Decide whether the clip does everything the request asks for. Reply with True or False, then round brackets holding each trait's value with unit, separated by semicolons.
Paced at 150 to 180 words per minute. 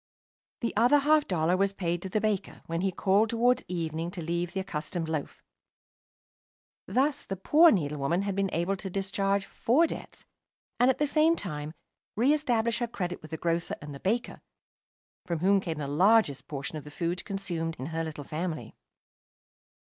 True (175 wpm)